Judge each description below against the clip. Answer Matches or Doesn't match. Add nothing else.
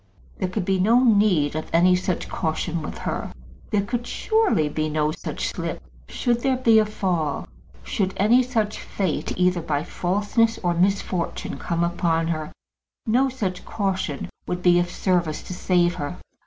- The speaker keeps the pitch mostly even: Doesn't match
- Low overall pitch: Doesn't match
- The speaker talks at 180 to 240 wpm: Doesn't match